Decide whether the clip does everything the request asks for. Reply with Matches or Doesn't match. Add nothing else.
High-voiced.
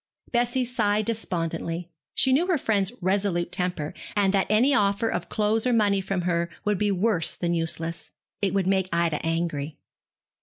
Matches